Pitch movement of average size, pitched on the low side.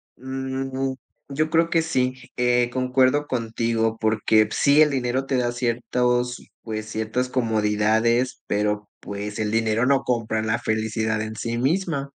Yes: average, 3.1 semitones; low, 120 Hz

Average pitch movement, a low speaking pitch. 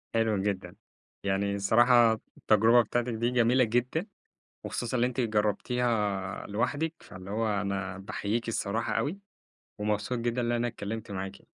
Yes: average, 3.1 semitones; low, 110 Hz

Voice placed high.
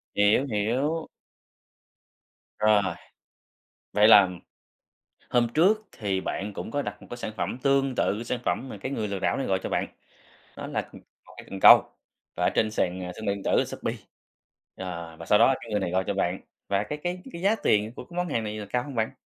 No: low, 110 Hz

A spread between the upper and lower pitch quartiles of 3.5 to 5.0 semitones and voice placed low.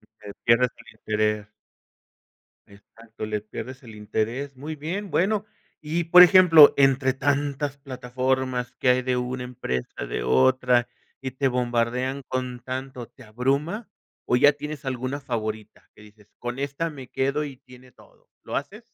No: average, 2.9 semitones; low, 130 Hz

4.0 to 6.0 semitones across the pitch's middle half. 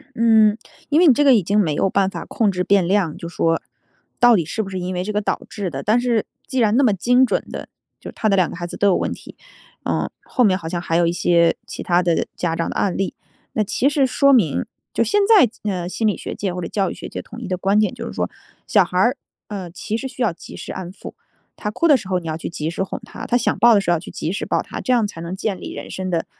Yes: average, 4.4 semitones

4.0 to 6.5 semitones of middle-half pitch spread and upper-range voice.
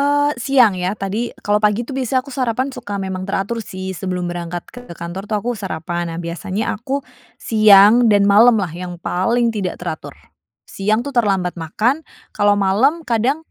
Yes: average, 4.4 semitones; high, 205 Hz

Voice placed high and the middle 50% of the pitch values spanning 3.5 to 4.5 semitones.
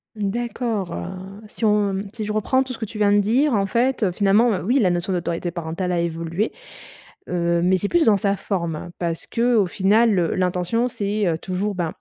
Yes: high, 200 Hz; average, 3.8 semitones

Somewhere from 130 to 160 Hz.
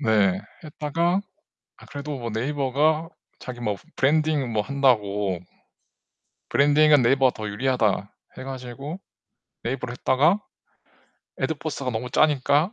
Yes: low, 135 Hz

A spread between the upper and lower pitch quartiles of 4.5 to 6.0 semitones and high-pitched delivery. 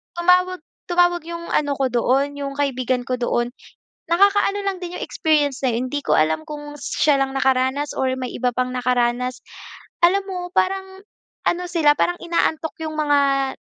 Yes: average, 5.1 semitones; very high, 290 Hz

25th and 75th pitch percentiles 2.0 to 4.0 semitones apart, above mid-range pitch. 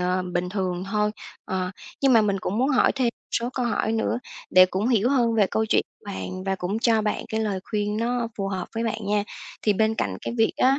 Yes: average, 3.3 semitones; high, 215 Hz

